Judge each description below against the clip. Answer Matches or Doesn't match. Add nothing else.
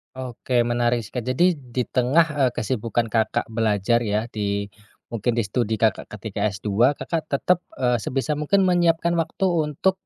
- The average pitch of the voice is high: Doesn't match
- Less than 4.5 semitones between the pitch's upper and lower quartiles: Doesn't match